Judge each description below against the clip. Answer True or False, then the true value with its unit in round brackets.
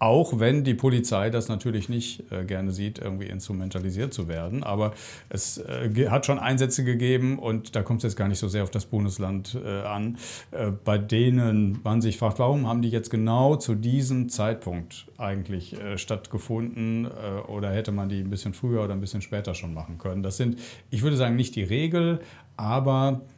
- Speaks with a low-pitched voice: True (110 Hz)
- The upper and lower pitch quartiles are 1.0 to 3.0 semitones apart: False (3.6 semitones)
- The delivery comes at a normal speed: False (200 wpm)